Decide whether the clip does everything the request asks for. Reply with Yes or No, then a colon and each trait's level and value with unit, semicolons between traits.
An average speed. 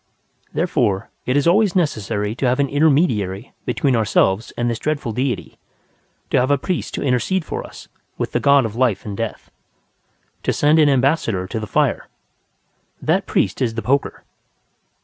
Yes: average, 170 wpm